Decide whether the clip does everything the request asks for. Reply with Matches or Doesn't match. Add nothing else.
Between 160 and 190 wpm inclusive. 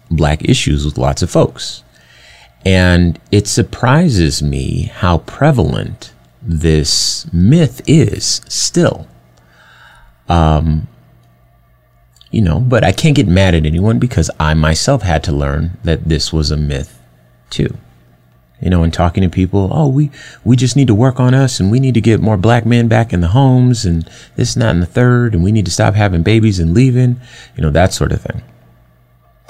Matches